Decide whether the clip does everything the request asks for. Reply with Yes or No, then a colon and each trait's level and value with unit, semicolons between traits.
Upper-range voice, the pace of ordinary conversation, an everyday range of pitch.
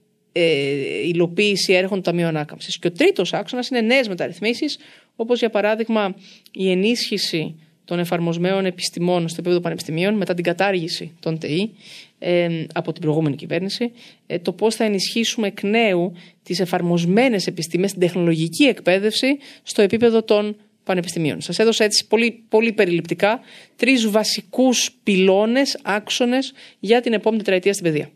Yes: high, 195 Hz; average, 145 wpm; average, 4.3 semitones